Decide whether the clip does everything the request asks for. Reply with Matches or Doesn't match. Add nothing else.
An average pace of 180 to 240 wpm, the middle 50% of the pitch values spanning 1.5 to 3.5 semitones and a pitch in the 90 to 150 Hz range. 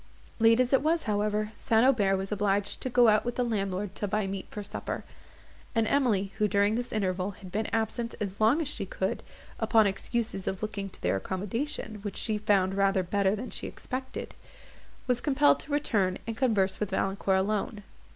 Doesn't match